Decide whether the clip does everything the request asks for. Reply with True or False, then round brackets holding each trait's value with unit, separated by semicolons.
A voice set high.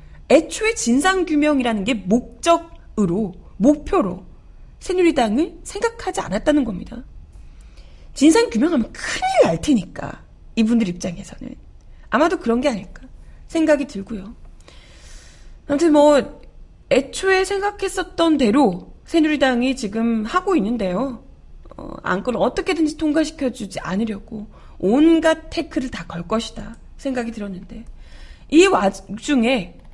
True (265 Hz)